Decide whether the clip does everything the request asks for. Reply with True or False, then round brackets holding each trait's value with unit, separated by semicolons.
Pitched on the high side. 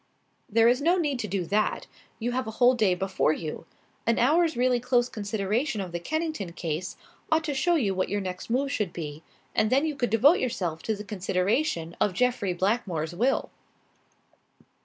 True (220 Hz)